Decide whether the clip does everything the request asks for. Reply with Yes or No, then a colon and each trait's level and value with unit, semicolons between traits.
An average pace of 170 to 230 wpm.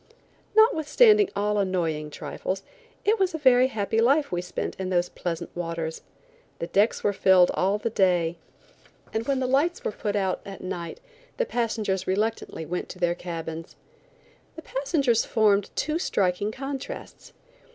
No: average, 150 wpm